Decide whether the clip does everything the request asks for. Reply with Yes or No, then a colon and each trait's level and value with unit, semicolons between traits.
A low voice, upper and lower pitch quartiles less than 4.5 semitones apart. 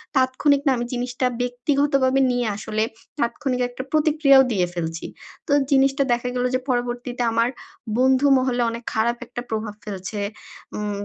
No: high, 245 Hz; narrow, 2.5 semitones